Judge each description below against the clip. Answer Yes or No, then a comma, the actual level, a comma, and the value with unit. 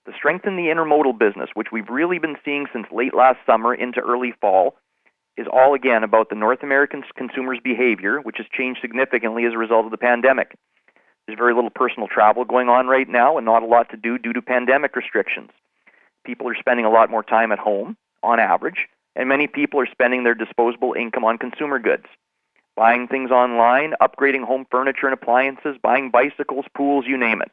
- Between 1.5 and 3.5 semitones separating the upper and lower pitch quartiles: Yes, narrow, 2.4 semitones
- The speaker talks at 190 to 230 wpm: Yes, average, 200 wpm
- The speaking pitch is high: No, low, 125 Hz